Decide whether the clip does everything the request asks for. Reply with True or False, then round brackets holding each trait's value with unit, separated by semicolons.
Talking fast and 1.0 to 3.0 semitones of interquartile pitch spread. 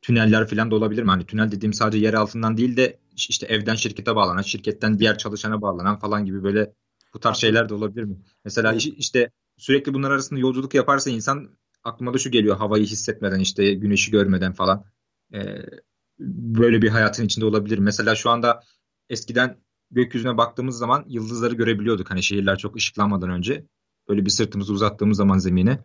True (170 wpm; 2.4 semitones)